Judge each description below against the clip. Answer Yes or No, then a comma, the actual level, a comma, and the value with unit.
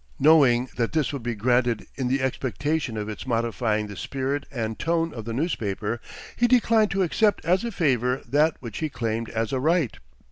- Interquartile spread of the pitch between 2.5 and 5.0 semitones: No, wide, 5.6 semitones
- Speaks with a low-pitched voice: Yes, low, 130 Hz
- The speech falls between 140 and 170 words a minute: No, average, 190 wpm